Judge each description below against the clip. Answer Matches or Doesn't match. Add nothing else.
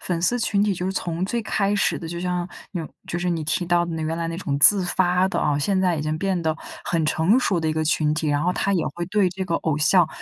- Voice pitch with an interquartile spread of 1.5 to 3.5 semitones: Matches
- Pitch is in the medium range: Matches